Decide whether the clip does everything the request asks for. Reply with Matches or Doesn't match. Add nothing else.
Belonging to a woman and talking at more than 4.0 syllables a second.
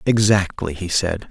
Doesn't match